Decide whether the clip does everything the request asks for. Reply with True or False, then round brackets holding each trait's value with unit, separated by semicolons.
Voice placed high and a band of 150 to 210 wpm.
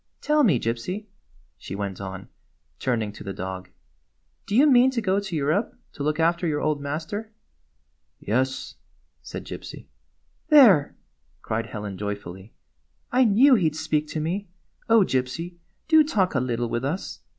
False (150 Hz; 170 wpm)